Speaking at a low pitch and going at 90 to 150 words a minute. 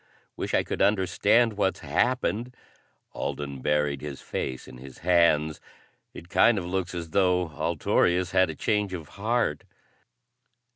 Yes: very low, 90 Hz; average, 140 wpm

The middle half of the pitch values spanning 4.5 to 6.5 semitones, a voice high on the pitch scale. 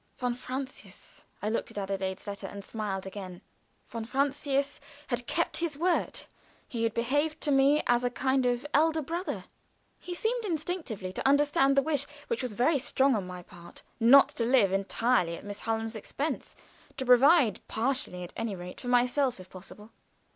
Yes: wide, 5.4 semitones; high, 245 Hz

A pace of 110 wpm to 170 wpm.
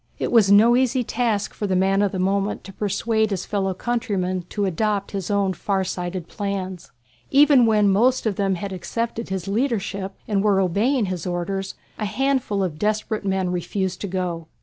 No: average, 185 wpm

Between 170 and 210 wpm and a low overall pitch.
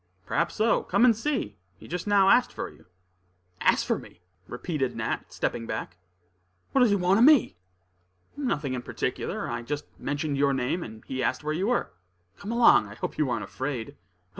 No: average, 190 wpm; medium, 150 Hz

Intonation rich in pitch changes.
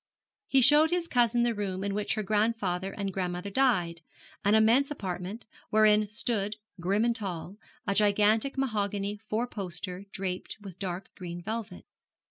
No: average, 3.2 semitones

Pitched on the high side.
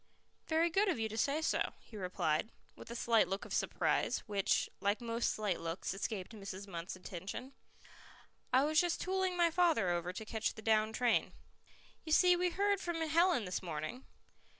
Yes: high, 225 Hz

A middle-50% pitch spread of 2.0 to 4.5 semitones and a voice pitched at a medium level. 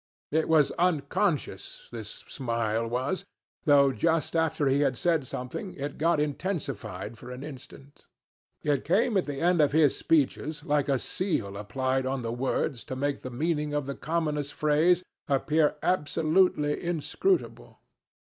Yes: average, 3.7 semitones; medium, 145 Hz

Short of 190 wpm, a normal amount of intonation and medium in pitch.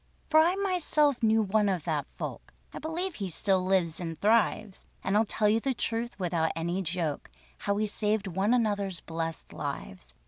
No: average, 180 wpm; average, 4.8 semitones; high, 200 Hz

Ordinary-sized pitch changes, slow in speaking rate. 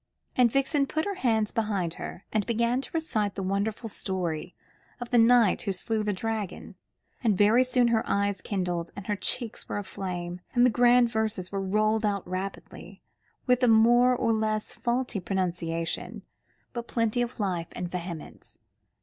No: average, 4.0 semitones; average, 165 wpm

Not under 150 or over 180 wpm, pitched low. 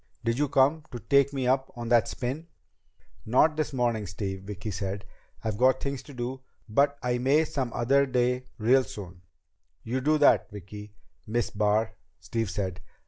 Yes: average, 170 wpm; low, 120 Hz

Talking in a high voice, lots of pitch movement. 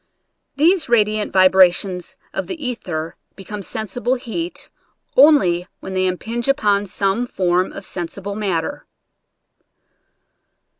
No: high, 200 Hz; average, 4.8 semitones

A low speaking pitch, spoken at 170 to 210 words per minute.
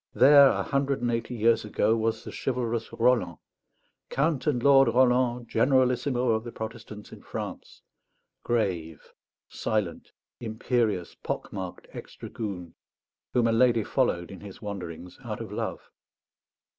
No: low, 115 Hz; slow, 135 wpm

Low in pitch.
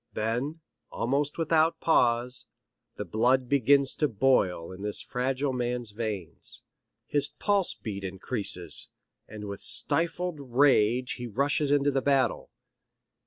Yes: low, 125 Hz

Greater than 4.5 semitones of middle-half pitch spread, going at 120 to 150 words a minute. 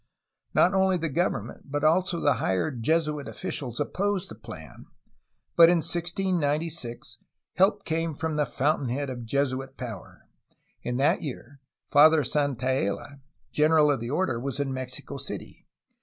No: average, 4.1 semitones; average, 140 wpm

